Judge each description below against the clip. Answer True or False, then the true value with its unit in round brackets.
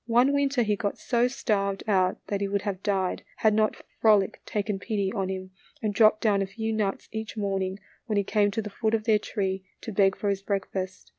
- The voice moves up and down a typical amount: False (2.1 semitones)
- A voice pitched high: True (205 Hz)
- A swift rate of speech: True (220 wpm)